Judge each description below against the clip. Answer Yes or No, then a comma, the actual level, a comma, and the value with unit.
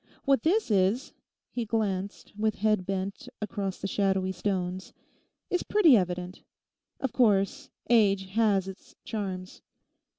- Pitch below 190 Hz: No, high, 200 Hz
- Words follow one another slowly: Yes, slow, 120 wpm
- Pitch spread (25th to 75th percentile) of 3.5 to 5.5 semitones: No, average, 3.1 semitones